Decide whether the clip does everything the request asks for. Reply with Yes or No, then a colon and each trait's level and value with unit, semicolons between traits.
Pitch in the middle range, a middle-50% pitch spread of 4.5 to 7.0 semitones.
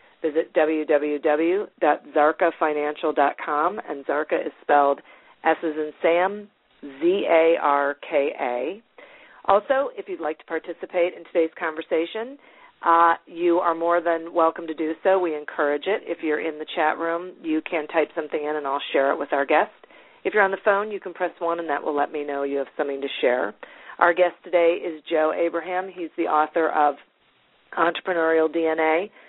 No: medium, 165 Hz; average, 2.7 semitones